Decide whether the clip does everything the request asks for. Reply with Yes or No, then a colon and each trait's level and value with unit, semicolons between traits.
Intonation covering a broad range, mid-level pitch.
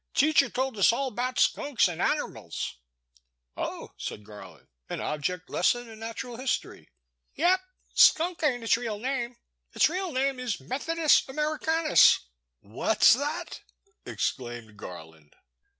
No: wide, 8.4 semitones; high, 245 Hz